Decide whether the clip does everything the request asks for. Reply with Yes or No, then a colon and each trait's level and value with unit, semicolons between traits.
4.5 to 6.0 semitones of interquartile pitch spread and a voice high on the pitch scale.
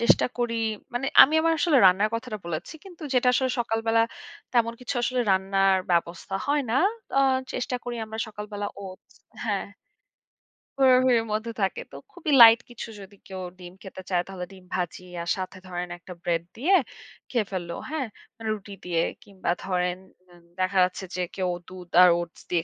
Yes: average, 4.8 semitones; high, 200 Hz